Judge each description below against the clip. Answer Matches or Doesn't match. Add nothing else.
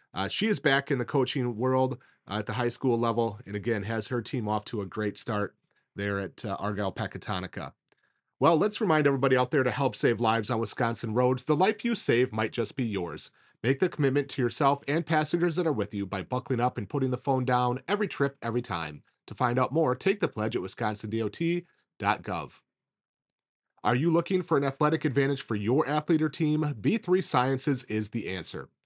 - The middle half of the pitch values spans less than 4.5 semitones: Doesn't match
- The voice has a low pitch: Matches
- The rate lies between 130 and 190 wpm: Doesn't match